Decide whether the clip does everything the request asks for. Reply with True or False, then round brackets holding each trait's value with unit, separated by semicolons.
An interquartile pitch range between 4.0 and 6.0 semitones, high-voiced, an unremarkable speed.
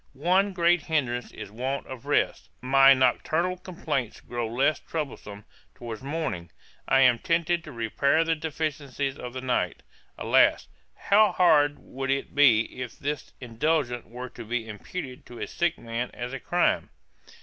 False (4.7 semitones; 135 Hz; 160 wpm)